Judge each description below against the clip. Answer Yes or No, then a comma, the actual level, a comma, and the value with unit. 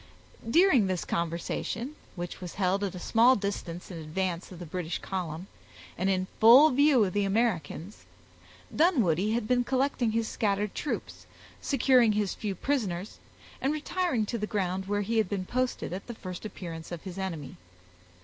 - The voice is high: Yes, high, 200 Hz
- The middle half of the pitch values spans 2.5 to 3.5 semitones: No, average, 4.8 semitones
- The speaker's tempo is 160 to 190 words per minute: Yes, average, 170 wpm